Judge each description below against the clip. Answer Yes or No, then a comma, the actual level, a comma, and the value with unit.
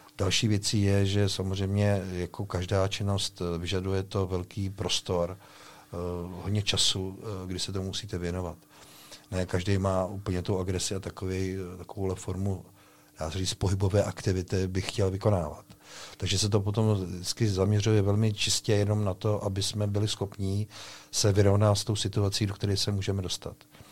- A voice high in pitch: No, low, 100 Hz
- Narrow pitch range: Yes, narrow, 1.8 semitones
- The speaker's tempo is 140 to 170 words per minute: Yes, average, 155 wpm